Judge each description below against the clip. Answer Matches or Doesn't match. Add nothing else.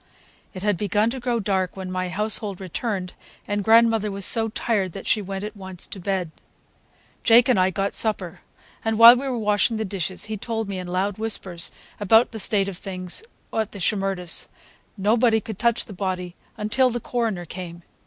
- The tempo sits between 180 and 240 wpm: Matches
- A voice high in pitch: Matches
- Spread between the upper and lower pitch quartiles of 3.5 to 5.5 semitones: Doesn't match